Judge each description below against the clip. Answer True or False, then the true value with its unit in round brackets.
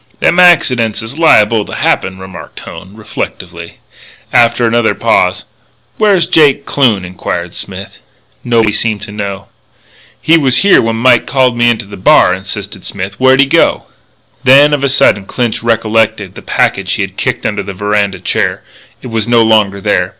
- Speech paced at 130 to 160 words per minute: False (170 wpm)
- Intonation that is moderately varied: True (4.4 semitones)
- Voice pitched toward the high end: False (110 Hz)